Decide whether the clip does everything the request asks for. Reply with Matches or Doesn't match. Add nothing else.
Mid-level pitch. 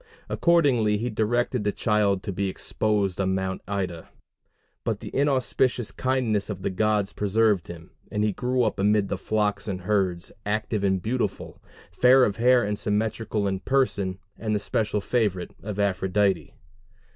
Doesn't match